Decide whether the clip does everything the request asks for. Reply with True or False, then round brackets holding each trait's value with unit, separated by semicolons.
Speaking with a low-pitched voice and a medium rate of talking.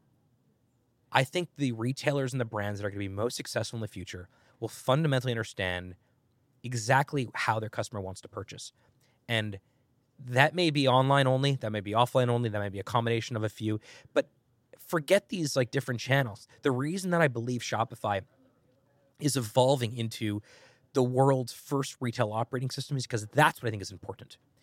True (125 Hz; 185 wpm)